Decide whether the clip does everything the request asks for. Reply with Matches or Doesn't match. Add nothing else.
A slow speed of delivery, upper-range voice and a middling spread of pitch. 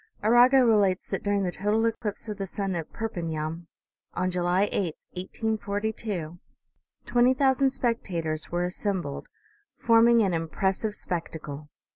Matches